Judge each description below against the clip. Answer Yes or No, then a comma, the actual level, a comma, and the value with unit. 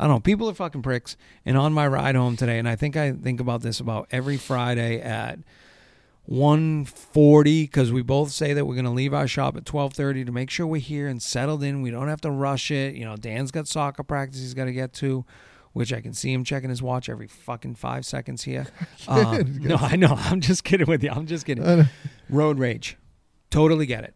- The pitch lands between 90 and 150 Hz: Yes, medium, 140 Hz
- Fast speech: Yes, fast, 230 wpm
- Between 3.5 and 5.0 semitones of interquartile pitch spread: No, average, 3.1 semitones